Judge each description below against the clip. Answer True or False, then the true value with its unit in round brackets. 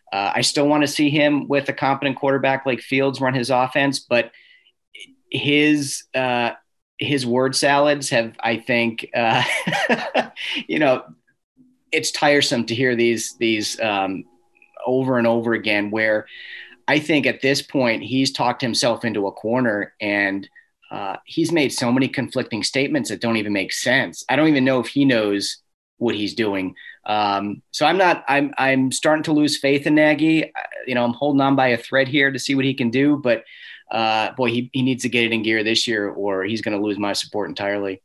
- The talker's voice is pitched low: True (130 Hz)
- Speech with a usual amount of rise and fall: True (4.0 semitones)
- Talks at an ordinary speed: True (195 wpm)